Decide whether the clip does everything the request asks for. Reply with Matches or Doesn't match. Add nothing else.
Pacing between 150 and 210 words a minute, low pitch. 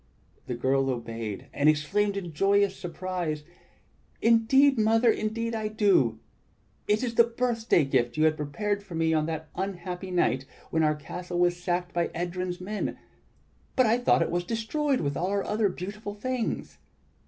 Doesn't match